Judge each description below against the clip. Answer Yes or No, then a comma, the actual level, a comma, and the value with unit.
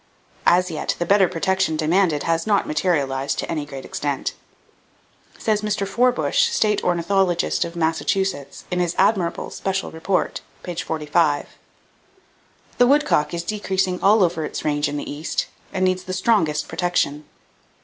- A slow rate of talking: No, average, 145 wpm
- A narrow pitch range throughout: No, average, 3.8 semitones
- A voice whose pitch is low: No, medium, 175 Hz